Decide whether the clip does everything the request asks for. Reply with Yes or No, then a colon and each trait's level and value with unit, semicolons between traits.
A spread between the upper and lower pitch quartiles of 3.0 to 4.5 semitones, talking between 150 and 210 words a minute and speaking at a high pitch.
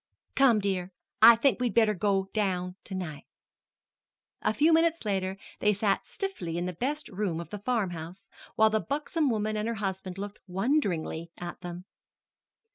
Yes: average, 4.2 semitones; average, 165 wpm; high, 200 Hz